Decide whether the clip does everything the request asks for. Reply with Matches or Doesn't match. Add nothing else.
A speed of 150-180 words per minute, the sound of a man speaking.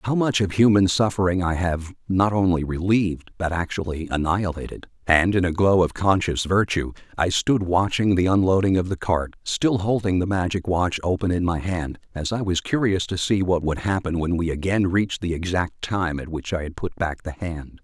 Doesn't match